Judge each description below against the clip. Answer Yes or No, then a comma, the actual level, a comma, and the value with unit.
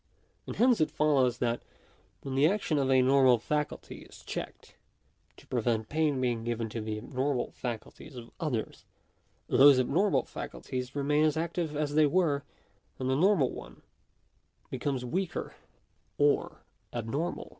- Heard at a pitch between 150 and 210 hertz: No, medium, 140 Hz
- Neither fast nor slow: Yes, average, 145 wpm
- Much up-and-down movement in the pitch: No, average, 3.7 semitones